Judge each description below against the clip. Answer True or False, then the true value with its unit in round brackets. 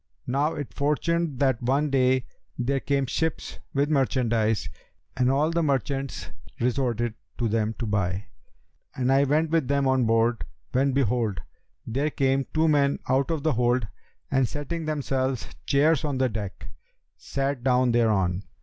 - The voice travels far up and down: False (3.0 semitones)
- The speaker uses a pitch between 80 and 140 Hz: True (135 Hz)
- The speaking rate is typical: True (150 wpm)